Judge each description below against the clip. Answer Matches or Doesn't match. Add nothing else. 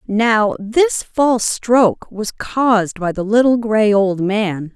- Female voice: Matches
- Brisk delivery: Doesn't match